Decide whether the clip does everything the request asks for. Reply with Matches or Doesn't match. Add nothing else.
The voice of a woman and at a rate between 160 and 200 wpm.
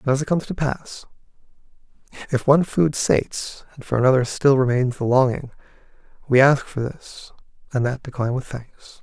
Doesn't match